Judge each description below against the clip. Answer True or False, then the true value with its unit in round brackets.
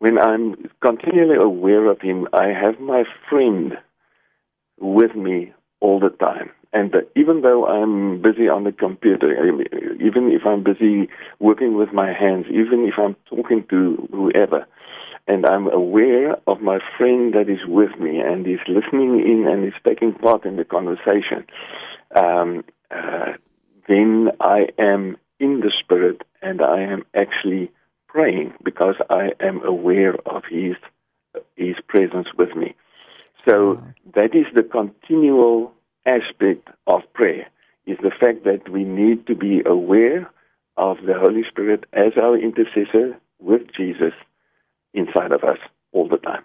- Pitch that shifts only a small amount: False (3.7 semitones)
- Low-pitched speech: True (110 Hz)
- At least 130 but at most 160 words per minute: True (145 wpm)